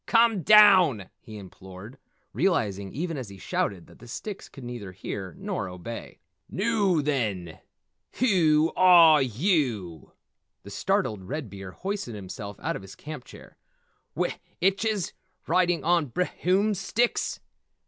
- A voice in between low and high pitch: Yes, medium, 145 Hz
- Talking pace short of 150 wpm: Yes, slow, 135 wpm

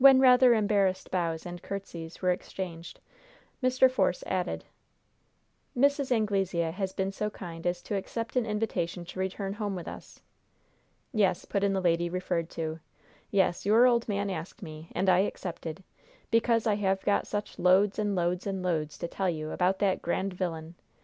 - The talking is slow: No, average, 170 wpm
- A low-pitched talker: No, high, 190 Hz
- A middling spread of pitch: Yes, average, 3.3 semitones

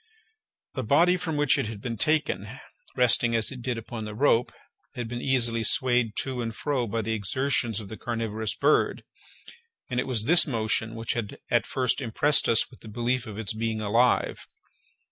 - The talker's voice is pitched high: No, low, 120 Hz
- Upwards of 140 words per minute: Yes, average, 185 wpm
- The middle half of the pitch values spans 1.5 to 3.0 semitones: Yes, average, 2.7 semitones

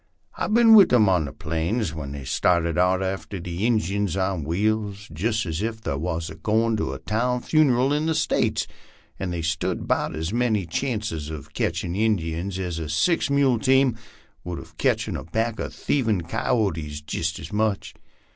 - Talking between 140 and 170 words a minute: No, average, 180 wpm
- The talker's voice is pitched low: Yes, low, 100 Hz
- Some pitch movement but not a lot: No, wide, 5.7 semitones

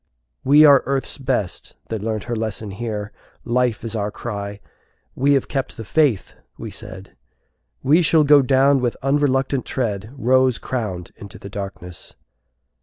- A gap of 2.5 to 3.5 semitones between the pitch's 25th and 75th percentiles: No, average, 4.7 semitones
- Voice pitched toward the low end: Yes, low, 120 Hz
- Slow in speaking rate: No, average, 150 wpm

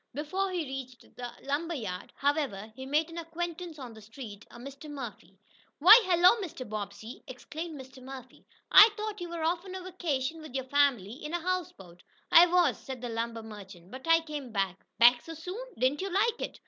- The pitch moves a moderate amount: No, wide, 6.1 semitones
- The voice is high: Yes, very high, 280 Hz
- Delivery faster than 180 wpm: Yes, average, 200 wpm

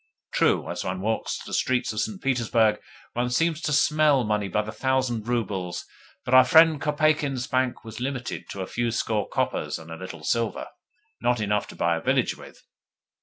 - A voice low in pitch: Yes, low, 120 Hz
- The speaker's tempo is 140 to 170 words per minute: No, average, 185 wpm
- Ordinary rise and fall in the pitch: Yes, average, 4.0 semitones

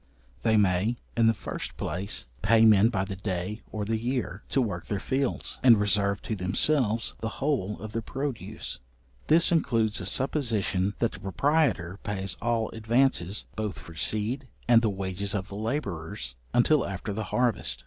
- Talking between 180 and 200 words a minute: No, average, 170 wpm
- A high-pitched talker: No, low, 110 Hz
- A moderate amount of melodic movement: Yes, average, 3.5 semitones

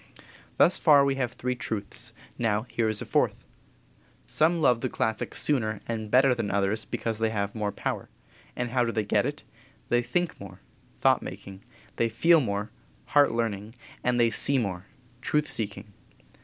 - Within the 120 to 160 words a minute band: No, average, 170 wpm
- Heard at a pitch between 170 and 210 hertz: No, low, 115 Hz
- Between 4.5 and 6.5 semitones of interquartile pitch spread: No, average, 3.4 semitones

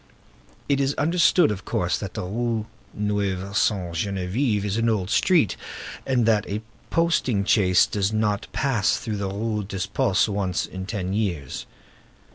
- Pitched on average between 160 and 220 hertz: No, low, 105 Hz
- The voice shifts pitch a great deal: No, average, 3.0 semitones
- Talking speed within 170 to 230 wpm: No, average, 155 wpm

